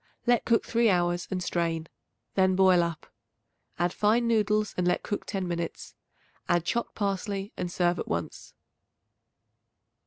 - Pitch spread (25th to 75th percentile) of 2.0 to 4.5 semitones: Yes, average, 3.2 semitones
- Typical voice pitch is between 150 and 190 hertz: Yes, medium, 185 Hz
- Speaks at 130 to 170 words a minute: Yes, average, 145 wpm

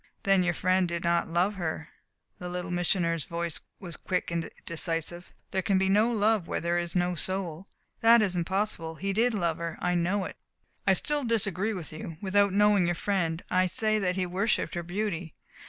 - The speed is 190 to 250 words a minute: Yes, average, 195 wpm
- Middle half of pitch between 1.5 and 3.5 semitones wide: Yes, average, 2.8 semitones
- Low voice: No, medium, 180 Hz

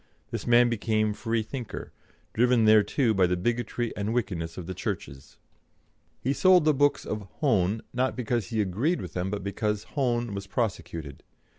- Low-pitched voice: Yes, low, 110 Hz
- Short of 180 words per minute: Yes, average, 165 wpm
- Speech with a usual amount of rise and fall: Yes, average, 3.7 semitones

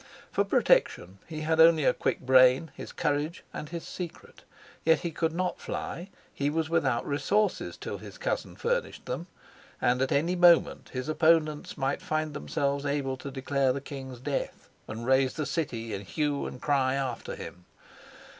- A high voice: No, medium, 145 Hz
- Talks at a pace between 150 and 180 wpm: Yes, average, 170 wpm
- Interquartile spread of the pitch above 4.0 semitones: No, average, 3.6 semitones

